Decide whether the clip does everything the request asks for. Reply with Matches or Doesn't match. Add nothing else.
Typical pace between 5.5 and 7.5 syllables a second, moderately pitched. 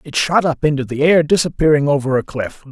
Matches